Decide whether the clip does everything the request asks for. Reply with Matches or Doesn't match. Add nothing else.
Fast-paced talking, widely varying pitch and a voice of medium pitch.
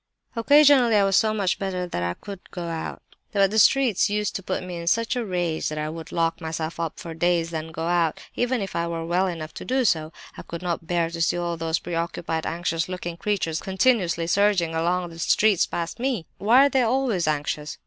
Doesn't match